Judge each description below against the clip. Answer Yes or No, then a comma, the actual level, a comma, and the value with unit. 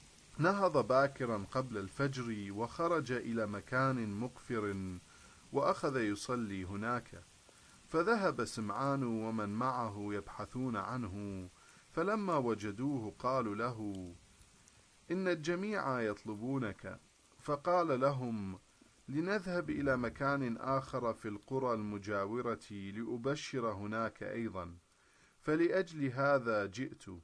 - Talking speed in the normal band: No, slow, 85 wpm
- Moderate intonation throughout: Yes, average, 4.8 semitones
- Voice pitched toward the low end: Yes, low, 115 Hz